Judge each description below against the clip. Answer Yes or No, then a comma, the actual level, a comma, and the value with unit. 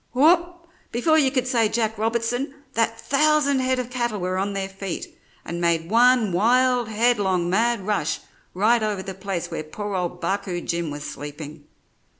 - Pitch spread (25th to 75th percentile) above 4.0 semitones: Yes, average, 5.2 semitones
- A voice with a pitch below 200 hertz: No, high, 220 Hz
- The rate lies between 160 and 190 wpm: Yes, average, 165 wpm